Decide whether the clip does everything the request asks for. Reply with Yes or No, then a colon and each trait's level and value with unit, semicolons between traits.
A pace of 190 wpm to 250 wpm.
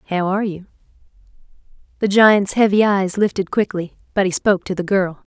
No: average, 170 wpm